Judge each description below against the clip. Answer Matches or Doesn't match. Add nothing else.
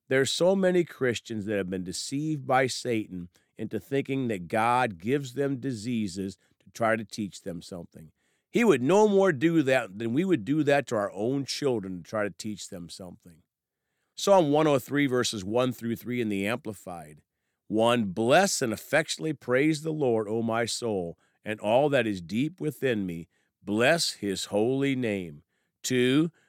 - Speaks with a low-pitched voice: Matches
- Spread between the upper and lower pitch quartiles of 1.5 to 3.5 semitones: Doesn't match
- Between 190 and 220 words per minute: Doesn't match